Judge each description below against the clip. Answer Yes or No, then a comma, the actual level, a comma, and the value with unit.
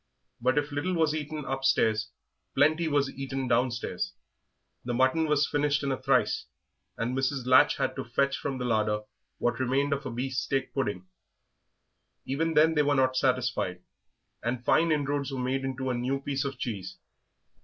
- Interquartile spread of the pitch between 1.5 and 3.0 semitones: Yes, narrow, 2.6 semitones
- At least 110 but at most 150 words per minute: No, average, 165 wpm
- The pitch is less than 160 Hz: Yes, low, 135 Hz